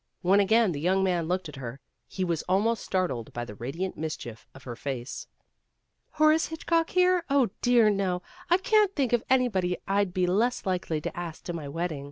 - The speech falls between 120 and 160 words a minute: No, average, 195 wpm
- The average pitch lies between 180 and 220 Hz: Yes, medium, 185 Hz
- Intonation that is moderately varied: No, wide, 7.1 semitones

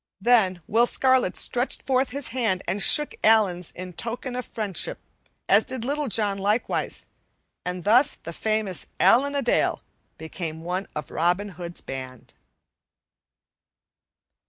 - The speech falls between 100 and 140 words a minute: Yes, slow, 135 wpm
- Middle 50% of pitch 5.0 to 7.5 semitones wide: Yes, wide, 5.4 semitones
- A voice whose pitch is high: Yes, high, 205 Hz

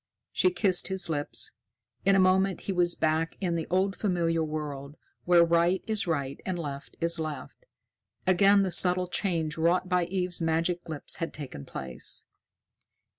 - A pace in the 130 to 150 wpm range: No, average, 160 wpm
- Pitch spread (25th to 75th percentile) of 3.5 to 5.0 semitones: No, narrow, 2.6 semitones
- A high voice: No, medium, 175 Hz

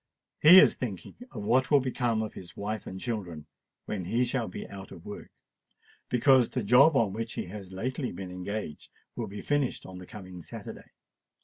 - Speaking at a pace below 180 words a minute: No, average, 185 wpm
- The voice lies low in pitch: Yes, low, 110 Hz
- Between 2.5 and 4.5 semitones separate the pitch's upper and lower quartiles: No, average, 5.0 semitones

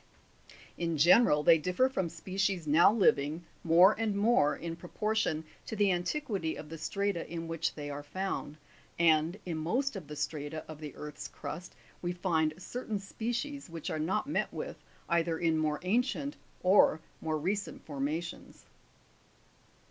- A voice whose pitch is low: No, medium, 170 Hz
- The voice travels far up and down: No, average, 4.2 semitones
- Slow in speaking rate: No, average, 155 wpm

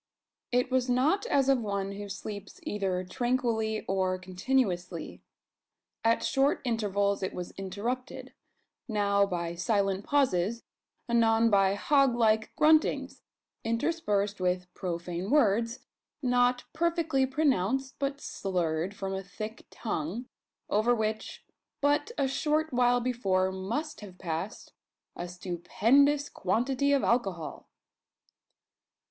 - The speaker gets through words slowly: Yes, slow, 115 wpm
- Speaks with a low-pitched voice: No, high, 220 Hz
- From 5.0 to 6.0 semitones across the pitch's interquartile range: Yes, average, 5.3 semitones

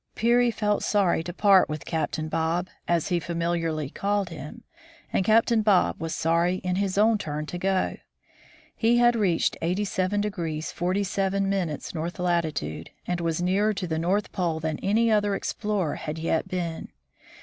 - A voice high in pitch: No, medium, 180 Hz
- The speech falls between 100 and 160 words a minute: Yes, average, 155 wpm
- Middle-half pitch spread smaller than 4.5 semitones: Yes, average, 3.8 semitones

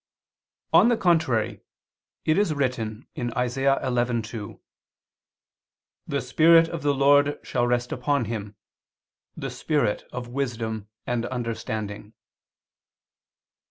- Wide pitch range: No, average, 4.0 semitones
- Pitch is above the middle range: No, low, 125 Hz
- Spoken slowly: Yes, slow, 100 wpm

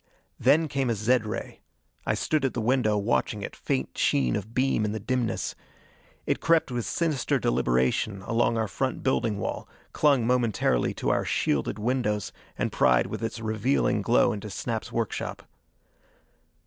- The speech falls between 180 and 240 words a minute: No, average, 160 wpm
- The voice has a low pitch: Yes, low, 115 Hz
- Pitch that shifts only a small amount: No, average, 3.5 semitones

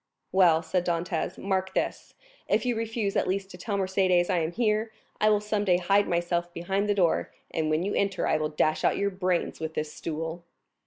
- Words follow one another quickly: Yes, fast, 210 wpm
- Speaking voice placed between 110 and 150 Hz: No, medium, 185 Hz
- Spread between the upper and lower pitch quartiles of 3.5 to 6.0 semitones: No, average, 2.9 semitones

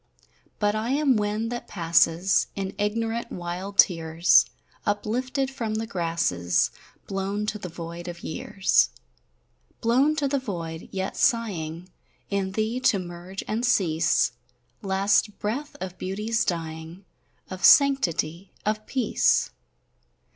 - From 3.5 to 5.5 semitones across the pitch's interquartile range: Yes, average, 4.7 semitones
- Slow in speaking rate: Yes, slow, 120 wpm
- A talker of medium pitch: No, high, 195 Hz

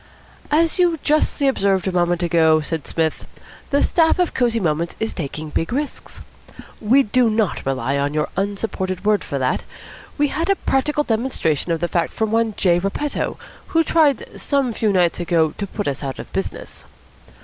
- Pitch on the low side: No, high, 200 Hz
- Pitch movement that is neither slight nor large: No, wide, 8.4 semitones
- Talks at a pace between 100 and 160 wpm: No, average, 180 wpm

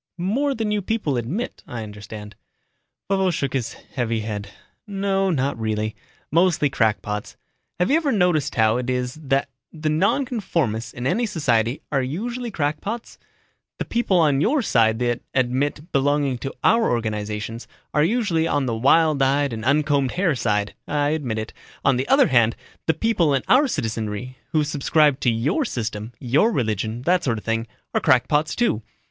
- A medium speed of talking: Yes, average, 165 wpm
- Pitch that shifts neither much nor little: No, wide, 7.5 semitones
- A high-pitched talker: No, medium, 140 Hz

